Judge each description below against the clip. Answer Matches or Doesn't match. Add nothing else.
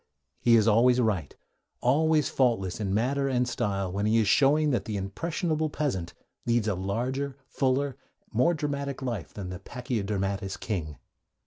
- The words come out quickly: Doesn't match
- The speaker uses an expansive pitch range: Matches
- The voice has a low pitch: Matches